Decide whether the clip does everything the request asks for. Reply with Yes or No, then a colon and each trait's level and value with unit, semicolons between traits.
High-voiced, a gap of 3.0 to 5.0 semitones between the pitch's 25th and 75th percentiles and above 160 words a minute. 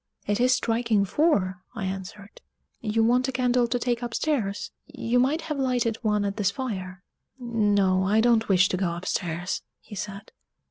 Yes: high, 220 Hz; average, 4.0 semitones; average, 170 wpm